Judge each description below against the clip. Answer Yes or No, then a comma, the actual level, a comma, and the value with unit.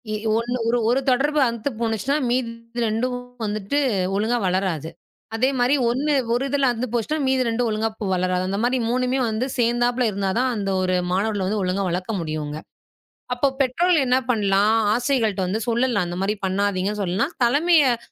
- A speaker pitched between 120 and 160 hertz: No, high, 230 Hz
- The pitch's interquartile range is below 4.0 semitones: No, average, 4.3 semitones